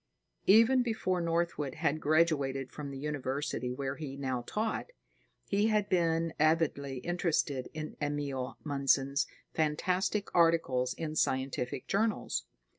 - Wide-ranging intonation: No, average, 4.0 semitones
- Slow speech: Yes, slow, 115 wpm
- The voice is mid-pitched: Yes, medium, 150 Hz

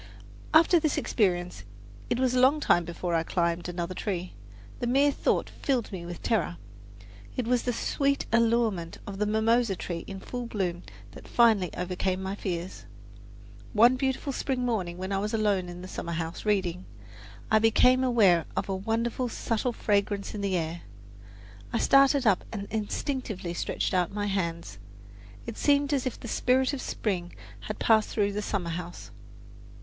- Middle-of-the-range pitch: No, high, 205 Hz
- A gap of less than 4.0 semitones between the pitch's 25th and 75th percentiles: No, average, 5.3 semitones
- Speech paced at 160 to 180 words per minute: Yes, average, 170 wpm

